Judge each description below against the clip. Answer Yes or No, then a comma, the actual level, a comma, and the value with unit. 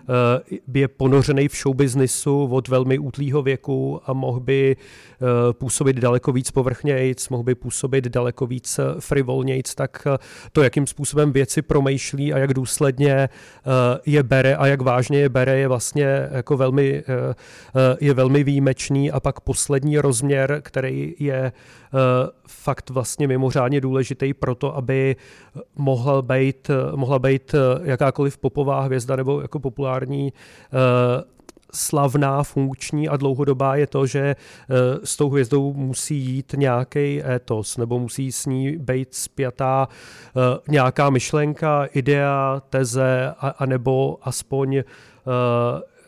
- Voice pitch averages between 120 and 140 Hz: Yes, low, 135 Hz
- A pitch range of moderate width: No, narrow, 1.5 semitones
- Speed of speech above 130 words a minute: No, average, 120 wpm